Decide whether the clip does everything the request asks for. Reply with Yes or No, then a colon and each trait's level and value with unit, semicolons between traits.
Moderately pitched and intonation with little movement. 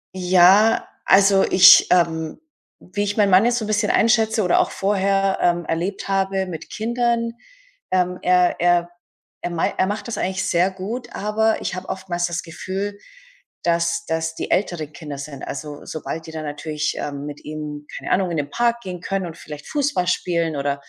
No: medium, 180 Hz; average, 3.8 semitones